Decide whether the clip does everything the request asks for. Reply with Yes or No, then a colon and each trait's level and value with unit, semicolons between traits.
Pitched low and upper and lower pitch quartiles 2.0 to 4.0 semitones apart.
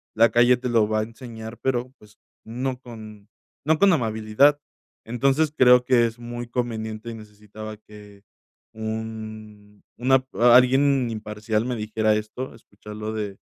Yes: low, 110 Hz; narrow, 2.6 semitones